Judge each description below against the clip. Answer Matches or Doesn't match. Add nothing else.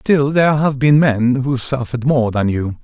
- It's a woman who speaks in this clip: Doesn't match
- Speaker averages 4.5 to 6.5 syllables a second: Matches